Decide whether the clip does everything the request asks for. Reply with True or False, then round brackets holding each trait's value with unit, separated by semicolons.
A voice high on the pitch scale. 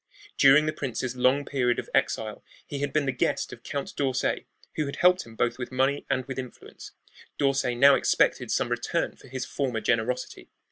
False (135 Hz)